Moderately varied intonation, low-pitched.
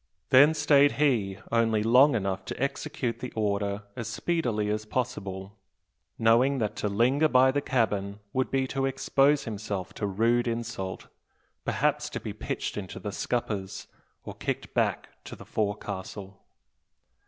Yes: average, 4.5 semitones; low, 115 Hz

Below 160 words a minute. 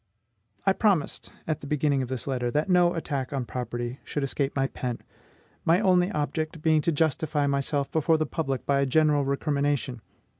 No: average, 180 wpm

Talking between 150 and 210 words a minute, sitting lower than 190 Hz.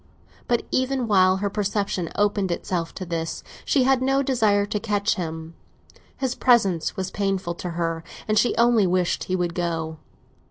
No: average, 165 wpm; high, 195 Hz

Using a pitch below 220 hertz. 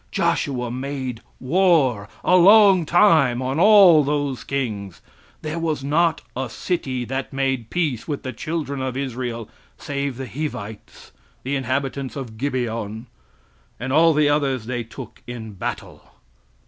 Yes: low, 135 Hz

